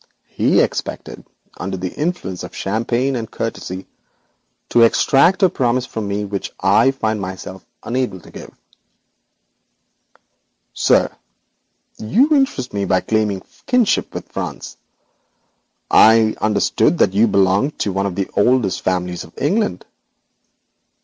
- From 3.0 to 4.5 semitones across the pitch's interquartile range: No, average, 5.1 semitones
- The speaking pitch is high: No, low, 110 Hz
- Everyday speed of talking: No, slow, 130 wpm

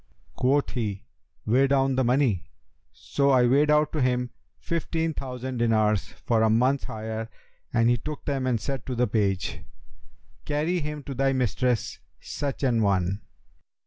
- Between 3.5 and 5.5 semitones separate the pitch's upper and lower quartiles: Yes, average, 3.8 semitones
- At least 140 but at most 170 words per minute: Yes, average, 155 wpm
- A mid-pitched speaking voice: No, low, 125 Hz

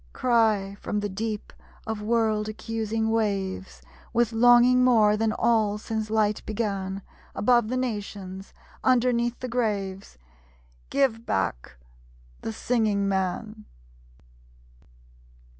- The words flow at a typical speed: No, slow, 105 wpm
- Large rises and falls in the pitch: No, narrow, 2.6 semitones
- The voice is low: No, high, 220 Hz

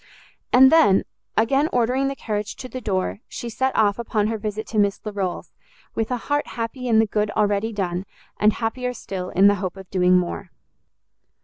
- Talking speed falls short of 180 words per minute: No, average, 190 wpm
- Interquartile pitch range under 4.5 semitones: Yes, average, 3.7 semitones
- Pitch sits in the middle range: No, high, 215 Hz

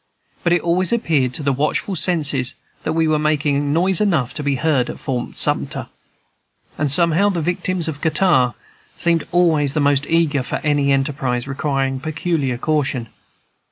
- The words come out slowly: No, average, 160 wpm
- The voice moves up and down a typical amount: Yes, average, 3.5 semitones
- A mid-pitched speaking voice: Yes, medium, 150 Hz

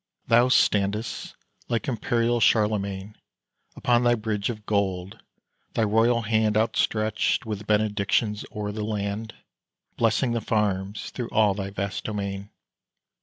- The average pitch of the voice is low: Yes, low, 105 Hz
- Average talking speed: No, slow, 125 wpm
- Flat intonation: Yes, narrow, 2.0 semitones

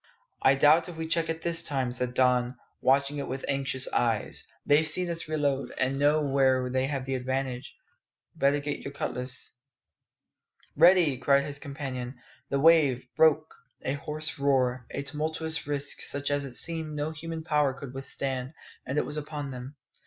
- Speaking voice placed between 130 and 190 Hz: Yes, medium, 140 Hz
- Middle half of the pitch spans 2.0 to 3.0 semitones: Yes, average, 2.7 semitones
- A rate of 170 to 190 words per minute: Yes, average, 175 wpm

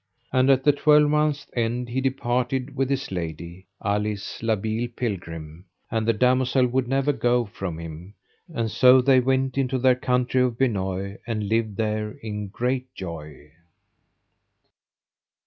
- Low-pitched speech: Yes, low, 120 Hz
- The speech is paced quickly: No, average, 145 wpm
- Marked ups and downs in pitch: No, average, 4.3 semitones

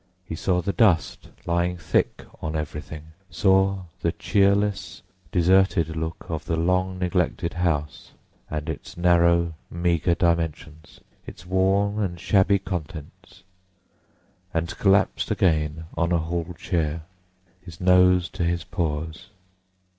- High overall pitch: No, very low, 85 Hz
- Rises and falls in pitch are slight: Yes, narrow, 2.3 semitones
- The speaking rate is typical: No, slow, 115 wpm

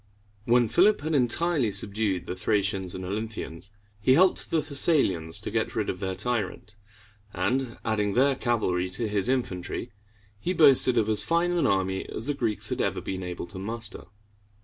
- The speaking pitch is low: Yes, low, 110 Hz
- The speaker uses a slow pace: No, average, 170 wpm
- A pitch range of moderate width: No, wide, 5.7 semitones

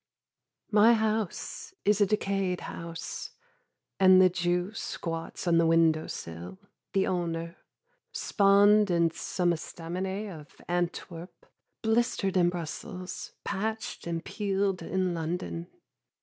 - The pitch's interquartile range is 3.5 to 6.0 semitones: No, average, 3.0 semitones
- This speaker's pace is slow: Yes, slow, 110 wpm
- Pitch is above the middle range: No, medium, 180 Hz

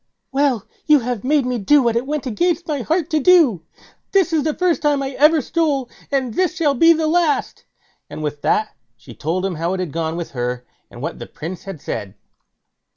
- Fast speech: Yes, fast, 215 wpm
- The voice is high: Yes, very high, 265 Hz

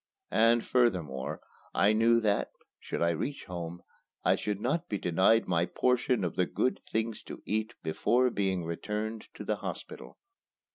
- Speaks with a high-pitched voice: No, low, 105 Hz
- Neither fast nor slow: Yes, average, 155 wpm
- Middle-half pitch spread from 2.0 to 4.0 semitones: No, average, 4.8 semitones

